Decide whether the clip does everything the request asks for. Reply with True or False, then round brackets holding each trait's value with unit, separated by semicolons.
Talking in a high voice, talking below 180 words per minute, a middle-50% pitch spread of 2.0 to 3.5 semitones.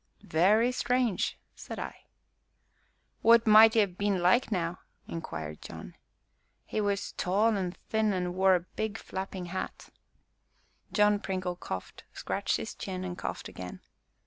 True (195 Hz; 140 wpm; 3.2 semitones)